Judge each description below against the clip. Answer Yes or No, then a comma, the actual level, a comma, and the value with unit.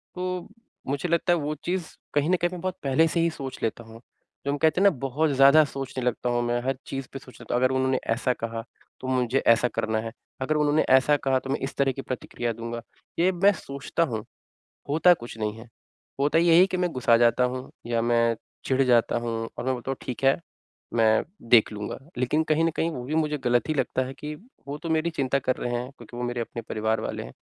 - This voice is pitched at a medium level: No, low, 130 Hz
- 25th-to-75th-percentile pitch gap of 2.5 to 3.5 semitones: No, average, 4.3 semitones